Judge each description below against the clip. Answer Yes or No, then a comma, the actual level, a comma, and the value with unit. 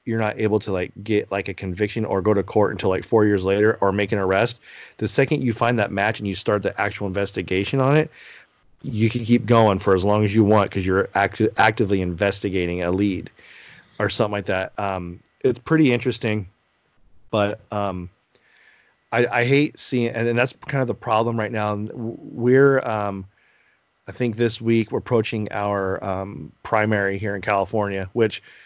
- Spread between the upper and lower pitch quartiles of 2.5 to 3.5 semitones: Yes, average, 2.9 semitones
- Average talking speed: Yes, average, 190 wpm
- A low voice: Yes, low, 105 Hz